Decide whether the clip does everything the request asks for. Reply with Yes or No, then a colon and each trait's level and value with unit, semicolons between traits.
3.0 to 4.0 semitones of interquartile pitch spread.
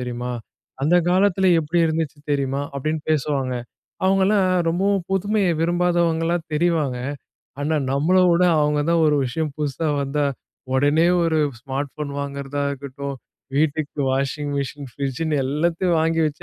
Yes: average, 3.3 semitones